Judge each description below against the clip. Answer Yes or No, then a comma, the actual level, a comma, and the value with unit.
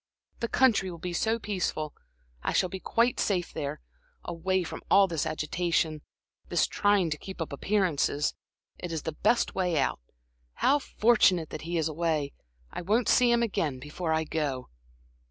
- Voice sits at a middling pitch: Yes, medium, 175 Hz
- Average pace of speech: Yes, average, 170 wpm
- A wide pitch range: No, average, 4.5 semitones